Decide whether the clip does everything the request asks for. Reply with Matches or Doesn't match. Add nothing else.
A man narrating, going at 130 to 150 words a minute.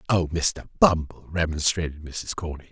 Matches